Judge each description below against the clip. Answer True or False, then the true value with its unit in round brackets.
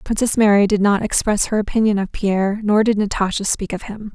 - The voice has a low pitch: False (205 Hz)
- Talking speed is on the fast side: True (215 wpm)